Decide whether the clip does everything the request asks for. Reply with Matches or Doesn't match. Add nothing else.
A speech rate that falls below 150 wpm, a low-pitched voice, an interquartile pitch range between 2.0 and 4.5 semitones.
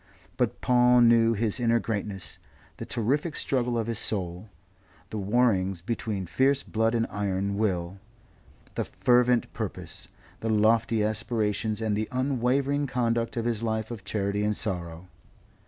Matches